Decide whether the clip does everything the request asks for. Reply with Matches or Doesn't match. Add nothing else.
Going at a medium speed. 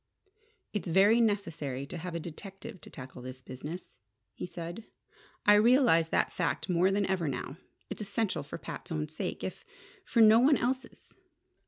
Matches